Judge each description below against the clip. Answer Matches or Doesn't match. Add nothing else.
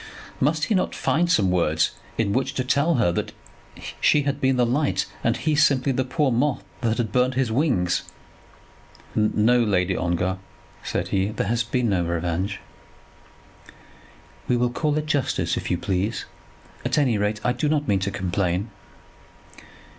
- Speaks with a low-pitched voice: Matches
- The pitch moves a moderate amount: Doesn't match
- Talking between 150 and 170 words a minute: Matches